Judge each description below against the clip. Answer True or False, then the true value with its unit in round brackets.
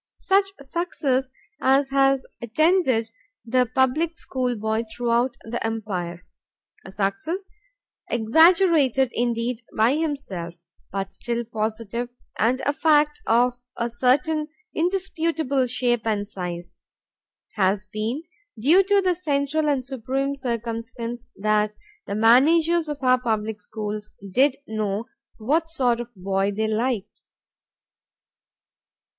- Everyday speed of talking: False (110 wpm)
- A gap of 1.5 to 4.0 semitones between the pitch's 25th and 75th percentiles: False (4.8 semitones)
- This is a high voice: True (245 Hz)